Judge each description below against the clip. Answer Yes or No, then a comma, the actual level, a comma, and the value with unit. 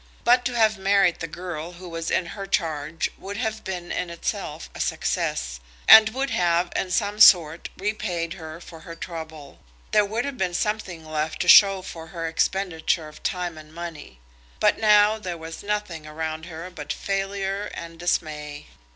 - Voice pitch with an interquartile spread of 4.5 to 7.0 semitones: No, average, 3.8 semitones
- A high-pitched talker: No, medium, 175 Hz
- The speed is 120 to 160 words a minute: No, average, 175 wpm